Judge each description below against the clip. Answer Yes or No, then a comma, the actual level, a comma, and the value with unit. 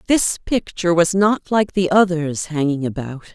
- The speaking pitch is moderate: Yes, medium, 175 Hz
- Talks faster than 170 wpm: No, average, 160 wpm